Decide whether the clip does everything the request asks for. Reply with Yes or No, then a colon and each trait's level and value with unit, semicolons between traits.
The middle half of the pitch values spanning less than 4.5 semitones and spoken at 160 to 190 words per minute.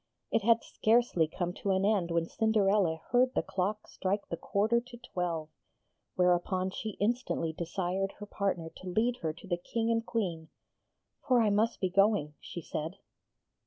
Yes: average, 4.1 semitones; average, 165 wpm